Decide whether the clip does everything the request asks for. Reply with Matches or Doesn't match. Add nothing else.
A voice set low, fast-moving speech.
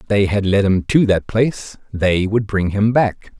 Matches